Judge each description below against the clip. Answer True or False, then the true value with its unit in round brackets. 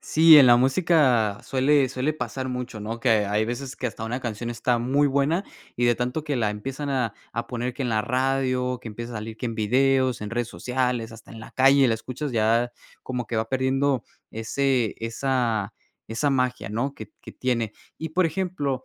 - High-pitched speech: False (125 Hz)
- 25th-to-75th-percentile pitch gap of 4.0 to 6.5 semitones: False (2.9 semitones)